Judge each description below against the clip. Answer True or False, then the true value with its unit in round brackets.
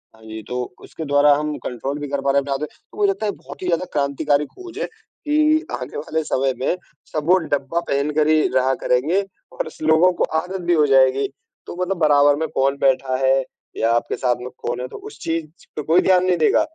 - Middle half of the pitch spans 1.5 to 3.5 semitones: False (4.3 semitones)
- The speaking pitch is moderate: True (145 Hz)